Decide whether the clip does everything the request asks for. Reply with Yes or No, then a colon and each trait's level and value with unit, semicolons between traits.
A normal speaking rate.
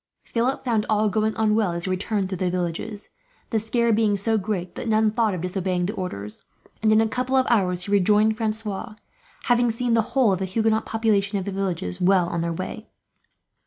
No: fast, 210 wpm